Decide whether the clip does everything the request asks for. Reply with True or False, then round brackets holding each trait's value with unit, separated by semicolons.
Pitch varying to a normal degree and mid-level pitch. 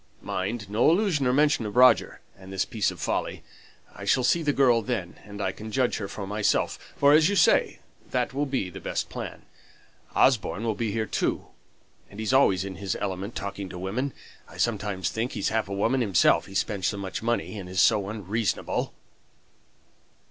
False (4.4 semitones; 110 Hz)